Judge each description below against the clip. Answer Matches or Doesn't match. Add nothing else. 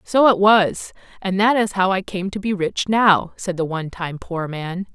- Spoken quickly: Matches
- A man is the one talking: Doesn't match